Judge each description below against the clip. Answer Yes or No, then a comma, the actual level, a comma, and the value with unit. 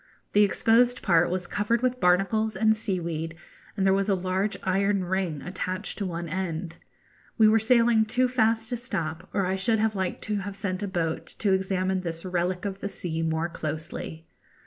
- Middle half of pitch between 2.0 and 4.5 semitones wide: Yes, average, 3.5 semitones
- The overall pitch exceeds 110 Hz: Yes, high, 190 Hz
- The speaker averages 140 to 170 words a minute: No, average, 190 wpm